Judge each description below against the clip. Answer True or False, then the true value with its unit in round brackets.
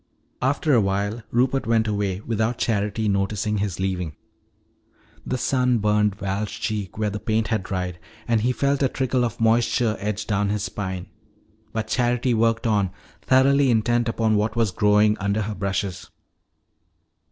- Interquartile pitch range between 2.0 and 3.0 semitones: True (2.7 semitones)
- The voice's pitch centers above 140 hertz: False (110 Hz)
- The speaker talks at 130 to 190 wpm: True (155 wpm)